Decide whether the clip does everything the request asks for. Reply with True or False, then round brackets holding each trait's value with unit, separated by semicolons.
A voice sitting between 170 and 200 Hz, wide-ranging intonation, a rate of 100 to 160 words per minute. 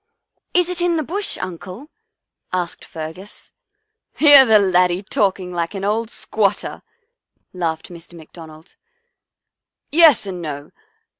True (190 Hz; 8.0 semitones; 145 wpm)